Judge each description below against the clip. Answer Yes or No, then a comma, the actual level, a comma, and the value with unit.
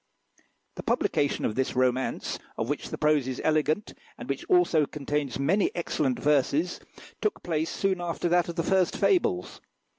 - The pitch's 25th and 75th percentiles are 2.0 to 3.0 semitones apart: No, average, 4.2 semitones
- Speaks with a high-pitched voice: No, medium, 155 Hz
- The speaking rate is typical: Yes, average, 160 wpm